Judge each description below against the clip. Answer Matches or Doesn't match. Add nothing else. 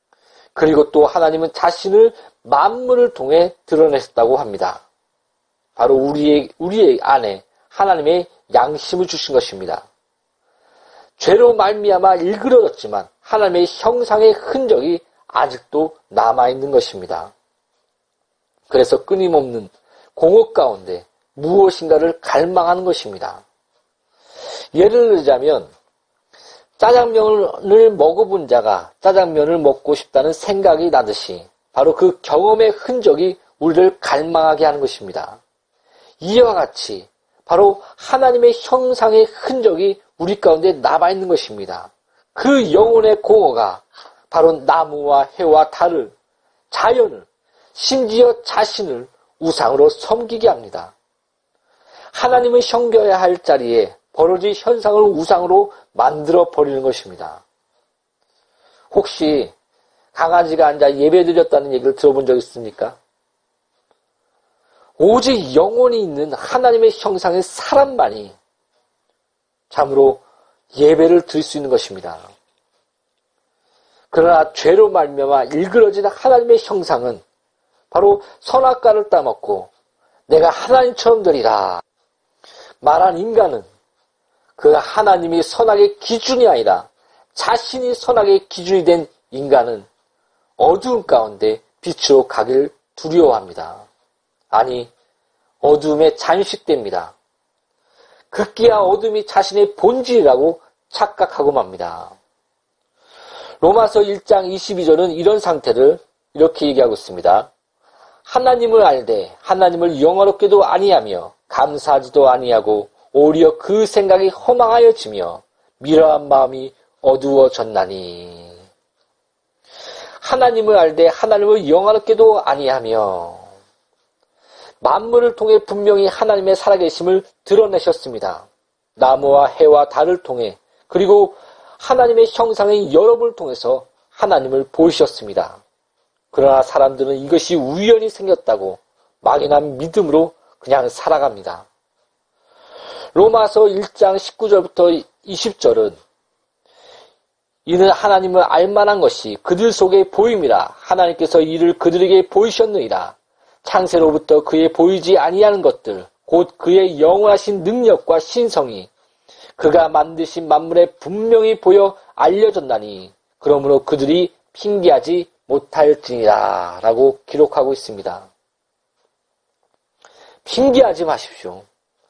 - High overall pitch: Matches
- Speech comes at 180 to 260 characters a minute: Matches